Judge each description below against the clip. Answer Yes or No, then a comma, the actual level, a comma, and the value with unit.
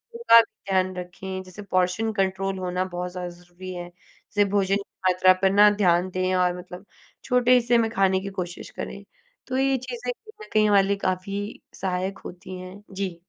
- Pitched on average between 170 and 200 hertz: Yes, high, 190 Hz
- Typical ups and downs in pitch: No, narrow, 2.3 semitones